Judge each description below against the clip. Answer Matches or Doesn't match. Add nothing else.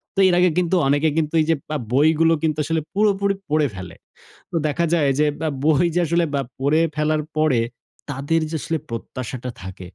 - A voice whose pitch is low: Doesn't match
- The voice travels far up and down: Doesn't match